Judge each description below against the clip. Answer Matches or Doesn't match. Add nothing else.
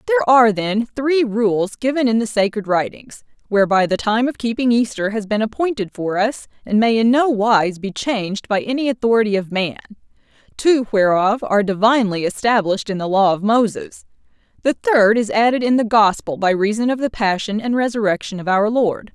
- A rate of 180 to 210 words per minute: Matches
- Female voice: Matches